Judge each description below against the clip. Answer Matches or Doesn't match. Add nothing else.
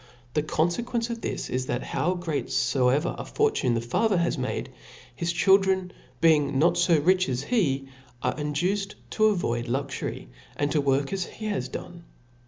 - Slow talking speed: Doesn't match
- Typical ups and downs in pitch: Doesn't match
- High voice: Doesn't match